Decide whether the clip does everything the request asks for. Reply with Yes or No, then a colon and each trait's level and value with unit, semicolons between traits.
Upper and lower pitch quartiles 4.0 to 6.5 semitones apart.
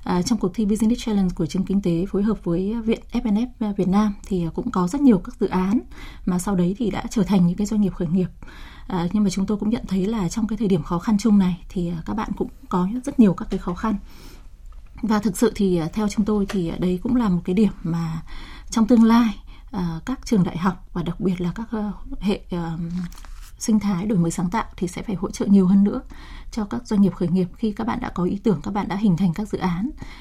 No: average, 3.3 semitones